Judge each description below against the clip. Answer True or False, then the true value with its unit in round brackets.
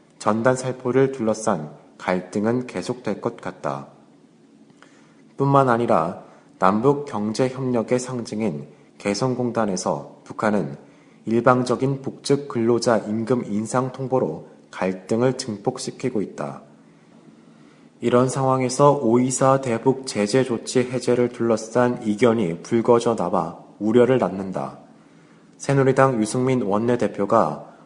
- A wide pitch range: False (3.3 semitones)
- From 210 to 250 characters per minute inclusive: True (240 characters per minute)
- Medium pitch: False (120 Hz)